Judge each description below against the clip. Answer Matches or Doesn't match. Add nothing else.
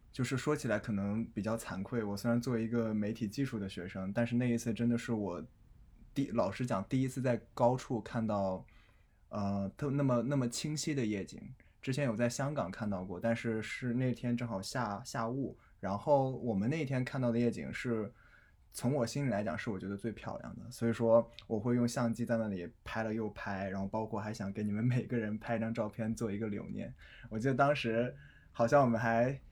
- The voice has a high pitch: Doesn't match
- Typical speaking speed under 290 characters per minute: Doesn't match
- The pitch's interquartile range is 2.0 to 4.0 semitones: Matches